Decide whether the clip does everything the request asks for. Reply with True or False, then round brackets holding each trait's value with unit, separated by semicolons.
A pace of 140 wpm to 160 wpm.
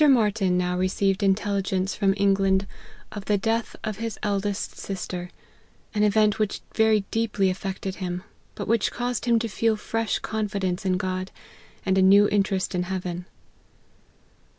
True (150 wpm)